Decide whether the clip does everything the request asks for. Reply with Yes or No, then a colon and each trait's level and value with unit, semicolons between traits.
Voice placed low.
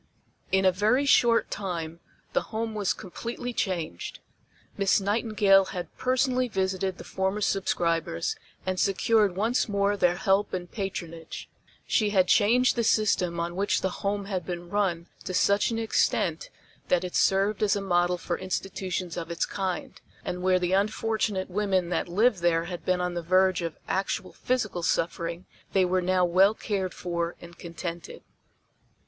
No: high, 190 Hz